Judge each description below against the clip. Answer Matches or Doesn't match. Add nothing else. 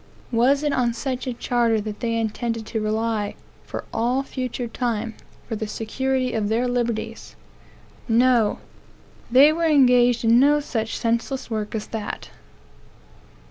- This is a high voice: Matches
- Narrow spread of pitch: Matches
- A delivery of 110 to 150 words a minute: Matches